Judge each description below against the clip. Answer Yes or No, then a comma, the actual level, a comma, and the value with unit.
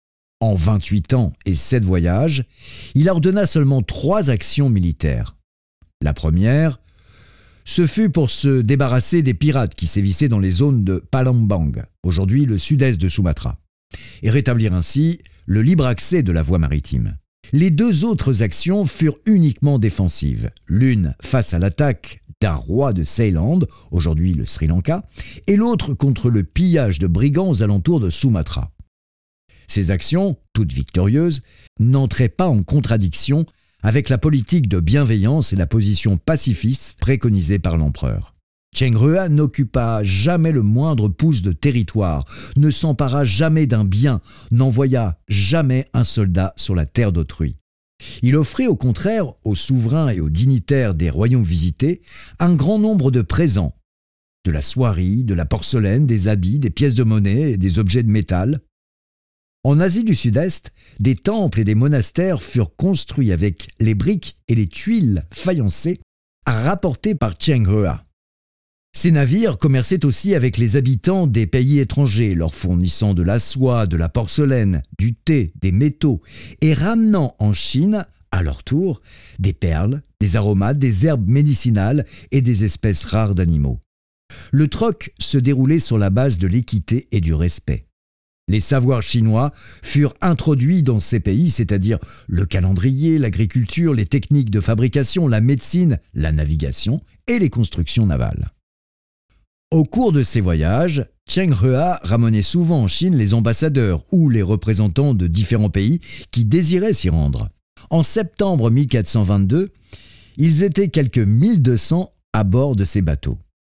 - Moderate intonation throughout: No, wide, 7.3 semitones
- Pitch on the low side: Yes, low, 115 Hz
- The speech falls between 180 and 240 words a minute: No, average, 150 wpm